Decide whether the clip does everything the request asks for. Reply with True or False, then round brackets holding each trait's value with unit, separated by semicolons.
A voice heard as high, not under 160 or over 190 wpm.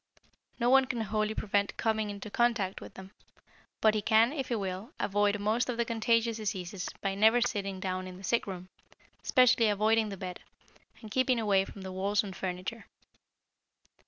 True (210 Hz; 180 wpm)